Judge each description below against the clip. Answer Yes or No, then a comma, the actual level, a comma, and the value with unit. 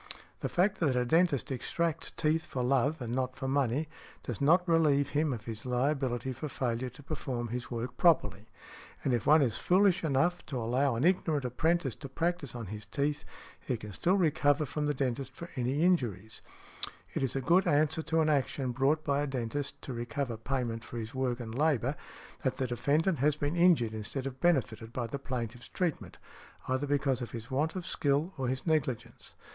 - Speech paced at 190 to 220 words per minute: Yes, average, 195 wpm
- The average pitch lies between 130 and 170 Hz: Yes, low, 135 Hz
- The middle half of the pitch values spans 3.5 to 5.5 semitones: Yes, average, 4.0 semitones